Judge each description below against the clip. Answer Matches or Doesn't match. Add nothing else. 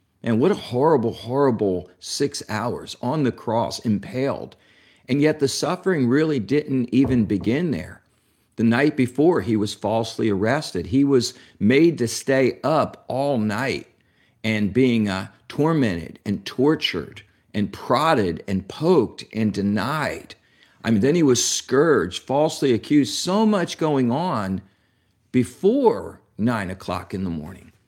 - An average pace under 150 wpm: Matches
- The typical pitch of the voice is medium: Doesn't match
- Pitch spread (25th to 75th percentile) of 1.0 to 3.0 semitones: Doesn't match